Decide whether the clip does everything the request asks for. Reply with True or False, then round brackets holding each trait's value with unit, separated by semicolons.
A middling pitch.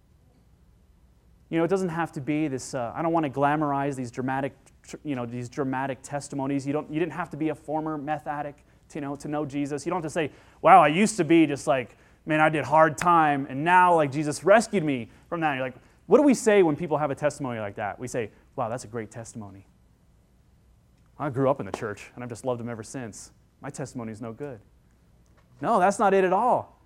True (145 Hz)